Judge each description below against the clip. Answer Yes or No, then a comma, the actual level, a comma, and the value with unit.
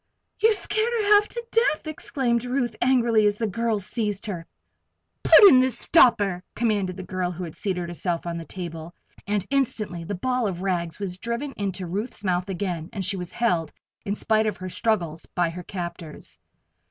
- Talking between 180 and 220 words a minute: Yes, average, 185 wpm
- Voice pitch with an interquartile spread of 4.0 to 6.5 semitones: Yes, average, 5.0 semitones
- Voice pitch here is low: No, high, 200 Hz